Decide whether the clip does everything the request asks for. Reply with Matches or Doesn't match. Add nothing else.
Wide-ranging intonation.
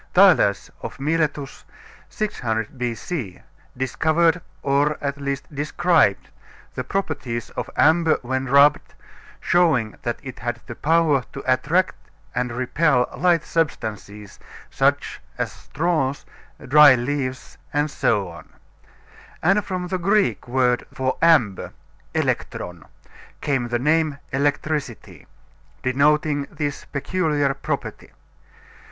Doesn't match